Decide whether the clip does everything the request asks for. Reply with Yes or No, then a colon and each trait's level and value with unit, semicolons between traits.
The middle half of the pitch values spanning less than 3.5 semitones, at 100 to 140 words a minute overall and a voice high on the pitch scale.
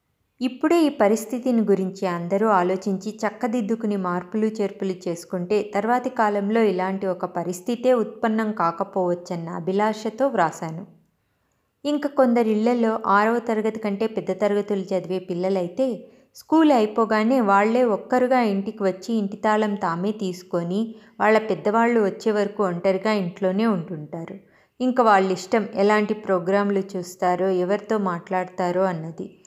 Yes: average, 3.1 semitones; average, 110 wpm; high, 205 Hz